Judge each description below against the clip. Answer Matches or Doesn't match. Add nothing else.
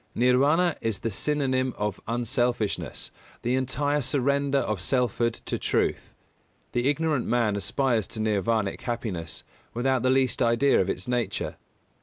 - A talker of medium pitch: Doesn't match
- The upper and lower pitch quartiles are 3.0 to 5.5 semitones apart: Matches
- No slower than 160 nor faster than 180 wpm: Doesn't match